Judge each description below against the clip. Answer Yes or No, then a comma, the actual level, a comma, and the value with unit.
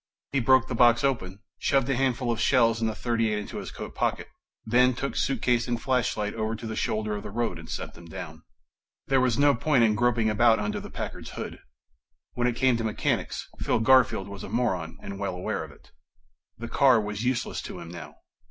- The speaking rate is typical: No, fast, 215 wpm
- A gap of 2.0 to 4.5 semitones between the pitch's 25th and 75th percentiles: Yes, average, 3.1 semitones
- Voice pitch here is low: Yes, low, 115 Hz